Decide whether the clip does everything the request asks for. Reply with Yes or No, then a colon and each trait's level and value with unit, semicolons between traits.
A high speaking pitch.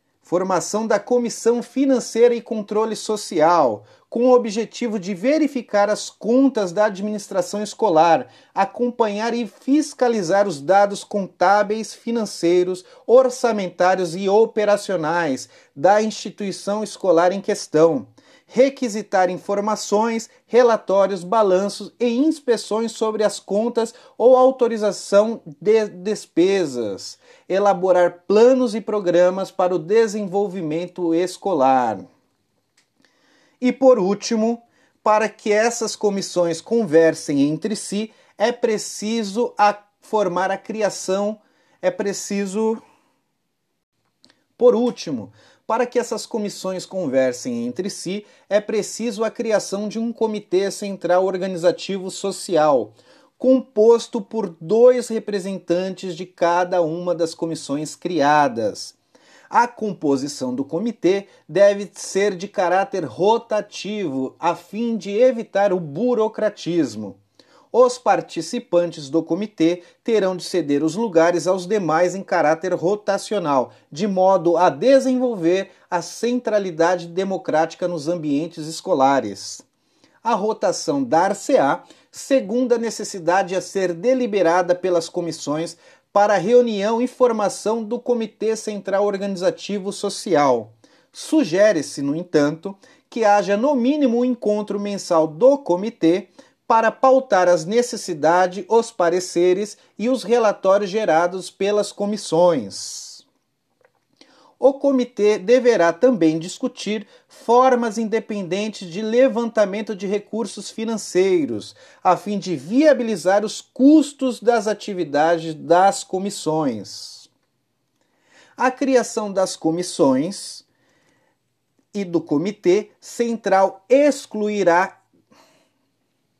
Yes: high, 205 Hz